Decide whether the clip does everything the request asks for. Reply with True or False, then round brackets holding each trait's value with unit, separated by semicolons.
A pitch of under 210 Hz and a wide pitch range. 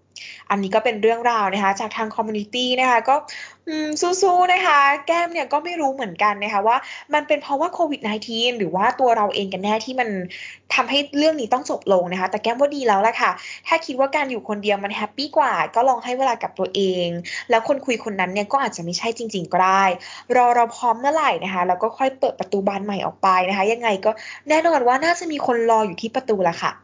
False (235 Hz; 5.7 semitones)